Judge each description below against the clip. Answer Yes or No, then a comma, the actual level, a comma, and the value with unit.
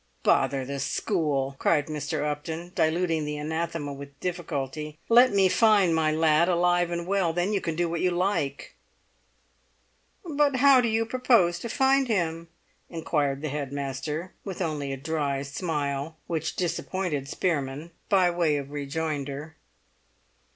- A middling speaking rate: Yes, average, 145 wpm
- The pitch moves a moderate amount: Yes, average, 3.8 semitones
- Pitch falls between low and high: Yes, medium, 160 Hz